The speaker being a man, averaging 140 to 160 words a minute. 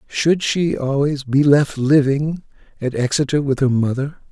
Yes: male; average, 155 wpm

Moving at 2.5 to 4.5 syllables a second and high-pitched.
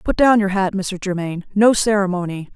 No: 5.6 syllables/s; high, 195 Hz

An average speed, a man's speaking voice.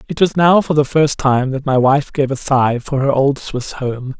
No: fast, 260 wpm; male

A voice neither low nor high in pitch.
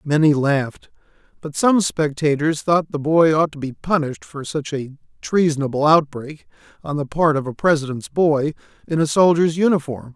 Yes: medium, 150 Hz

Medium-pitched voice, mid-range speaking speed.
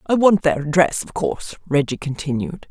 Yes: medium, 160 Hz; average, 175 wpm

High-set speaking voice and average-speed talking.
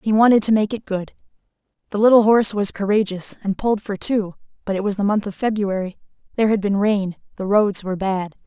No: high, 205 Hz; fast, 215 wpm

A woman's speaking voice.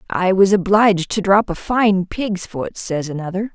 Yes: female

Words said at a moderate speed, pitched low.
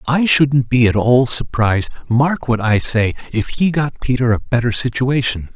Yes: average, 175 wpm; low, 125 Hz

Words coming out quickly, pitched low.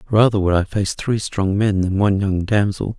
Yes: fast, 220 wpm; low, 100 Hz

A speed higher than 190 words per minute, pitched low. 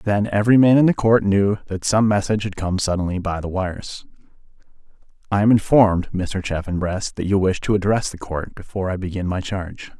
Yes: average, 200 wpm; low, 100 Hz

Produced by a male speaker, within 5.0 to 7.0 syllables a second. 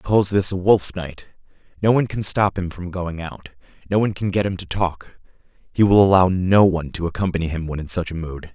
Yes: male; 5.9 syllables/s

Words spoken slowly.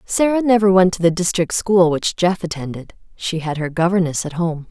No: fast, 205 wpm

